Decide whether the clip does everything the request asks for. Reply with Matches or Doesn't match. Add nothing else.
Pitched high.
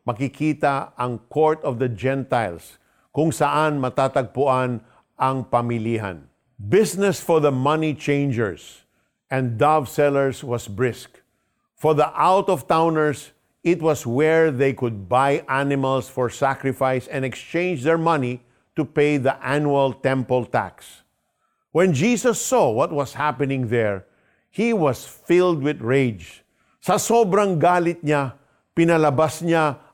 Doesn't match